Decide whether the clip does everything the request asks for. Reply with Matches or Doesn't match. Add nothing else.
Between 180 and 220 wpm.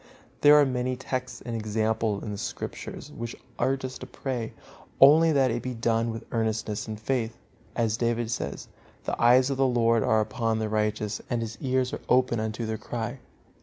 Matches